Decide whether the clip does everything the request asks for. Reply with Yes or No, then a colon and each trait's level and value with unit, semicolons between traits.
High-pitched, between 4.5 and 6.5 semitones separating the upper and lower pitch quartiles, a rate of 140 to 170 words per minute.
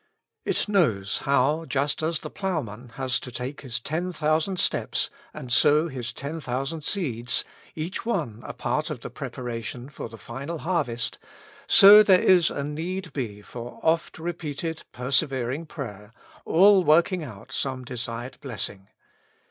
No: medium, 140 Hz; average, 5.2 semitones; average, 150 wpm